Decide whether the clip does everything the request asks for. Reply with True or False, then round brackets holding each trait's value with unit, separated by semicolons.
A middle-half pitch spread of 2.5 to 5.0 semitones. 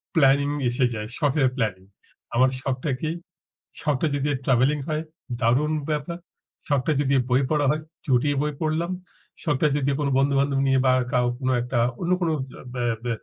True (2.8 semitones)